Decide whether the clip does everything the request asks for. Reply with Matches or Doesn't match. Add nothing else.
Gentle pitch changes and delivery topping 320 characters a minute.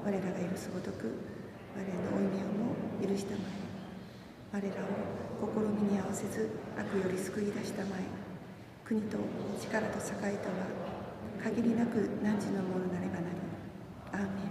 Doesn't match